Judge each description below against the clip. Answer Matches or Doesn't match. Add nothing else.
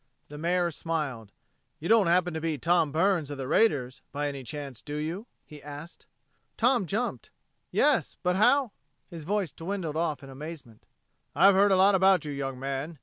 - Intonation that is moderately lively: Matches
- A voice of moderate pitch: Matches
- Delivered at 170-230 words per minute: Matches